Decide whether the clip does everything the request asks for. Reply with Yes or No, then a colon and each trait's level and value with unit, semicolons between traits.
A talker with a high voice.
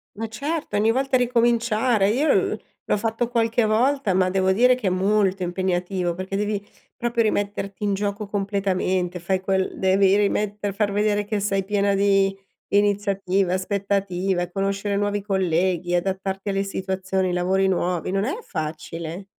Yes: high, 195 Hz